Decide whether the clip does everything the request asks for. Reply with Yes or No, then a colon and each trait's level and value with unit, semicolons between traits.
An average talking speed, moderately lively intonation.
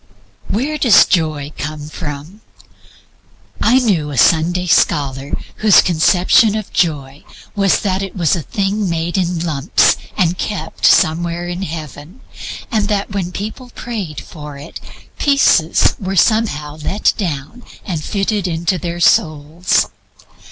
No: slow, 130 wpm; average, 4.6 semitones